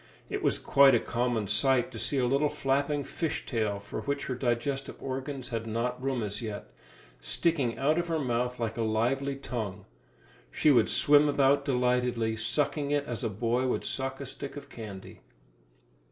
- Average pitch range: Yes, average, 3.4 semitones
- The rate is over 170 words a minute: Yes, average, 180 wpm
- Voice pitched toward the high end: No, low, 125 Hz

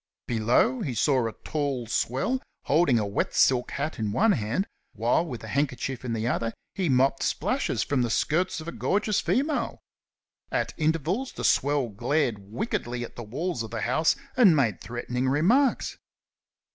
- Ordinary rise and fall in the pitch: No, wide, 6.0 semitones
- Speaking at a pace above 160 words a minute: Yes, average, 170 wpm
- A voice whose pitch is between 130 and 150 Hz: Yes, low, 135 Hz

